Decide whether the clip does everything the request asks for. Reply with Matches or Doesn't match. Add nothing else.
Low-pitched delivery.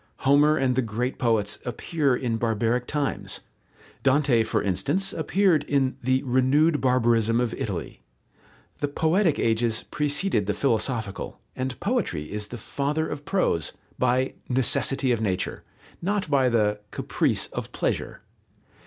Matches